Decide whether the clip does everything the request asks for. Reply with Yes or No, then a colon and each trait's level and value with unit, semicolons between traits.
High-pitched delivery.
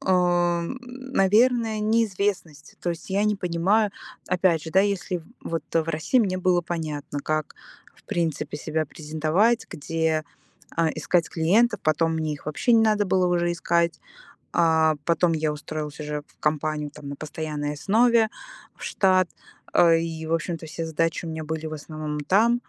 No: medium, 165 Hz